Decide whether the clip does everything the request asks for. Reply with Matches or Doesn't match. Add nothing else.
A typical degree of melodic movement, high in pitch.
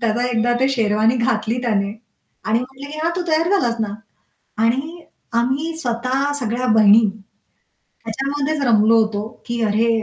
Matches